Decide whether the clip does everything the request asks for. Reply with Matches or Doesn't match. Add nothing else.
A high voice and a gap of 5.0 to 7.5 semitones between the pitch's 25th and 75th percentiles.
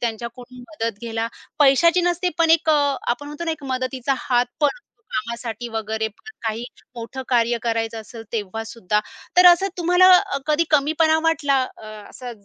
Matches